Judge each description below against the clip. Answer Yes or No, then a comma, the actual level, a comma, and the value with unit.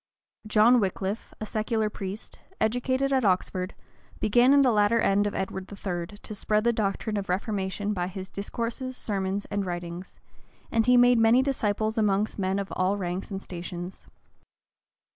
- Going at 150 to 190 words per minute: Yes, average, 160 wpm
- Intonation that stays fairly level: No, average, 3.0 semitones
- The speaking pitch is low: No, high, 205 Hz